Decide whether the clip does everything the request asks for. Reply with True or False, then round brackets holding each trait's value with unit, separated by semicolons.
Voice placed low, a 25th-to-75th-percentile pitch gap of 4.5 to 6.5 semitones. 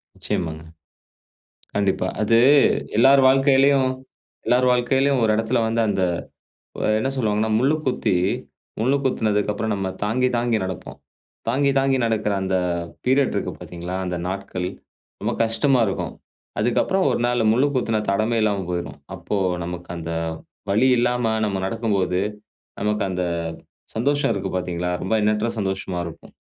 True (110 Hz; 4.8 semitones)